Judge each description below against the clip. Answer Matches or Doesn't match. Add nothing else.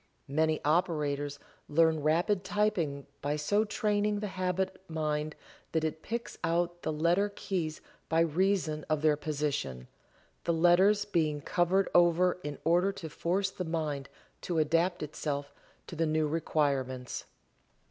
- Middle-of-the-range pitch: Matches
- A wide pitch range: Doesn't match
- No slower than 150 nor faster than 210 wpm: Doesn't match